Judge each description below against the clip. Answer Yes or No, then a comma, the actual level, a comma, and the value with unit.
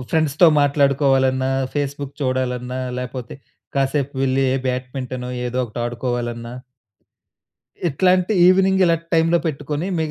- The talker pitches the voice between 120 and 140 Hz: Yes, low, 135 Hz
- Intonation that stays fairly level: No, average, 3.4 semitones